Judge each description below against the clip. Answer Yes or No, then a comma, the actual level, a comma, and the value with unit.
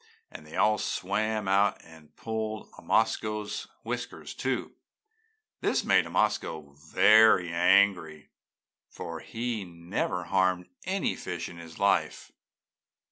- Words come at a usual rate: No, slow, 110 wpm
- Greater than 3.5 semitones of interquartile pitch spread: Yes, average, 4.2 semitones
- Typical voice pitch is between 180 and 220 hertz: No, very low, 95 Hz